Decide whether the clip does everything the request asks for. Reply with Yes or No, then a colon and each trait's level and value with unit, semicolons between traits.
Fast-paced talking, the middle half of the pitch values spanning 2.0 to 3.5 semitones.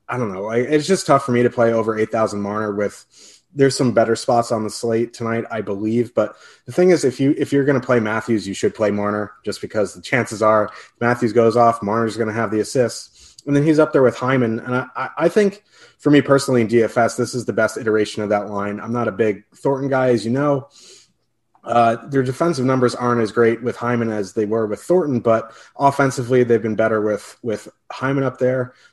Yes: fast, 230 wpm; average, 3.0 semitones